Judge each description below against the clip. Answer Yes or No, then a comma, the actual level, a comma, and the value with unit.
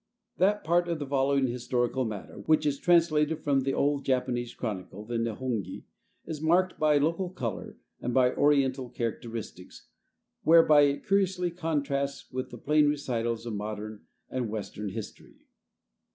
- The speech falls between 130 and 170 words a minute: Yes, average, 145 wpm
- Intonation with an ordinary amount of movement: Yes, average, 4.6 semitones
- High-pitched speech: No, low, 135 Hz